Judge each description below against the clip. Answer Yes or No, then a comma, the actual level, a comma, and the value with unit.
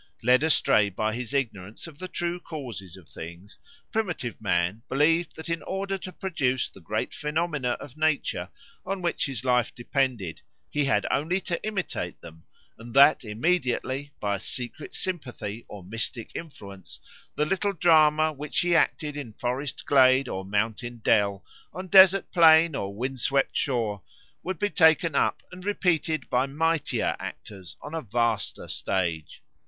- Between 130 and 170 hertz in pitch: Yes, low, 135 Hz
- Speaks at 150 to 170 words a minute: Yes, average, 155 wpm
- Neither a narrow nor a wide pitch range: No, wide, 7.0 semitones